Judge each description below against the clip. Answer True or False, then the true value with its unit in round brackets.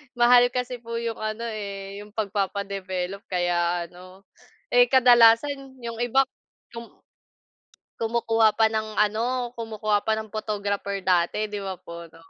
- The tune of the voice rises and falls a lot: False (2.9 semitones)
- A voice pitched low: False (215 Hz)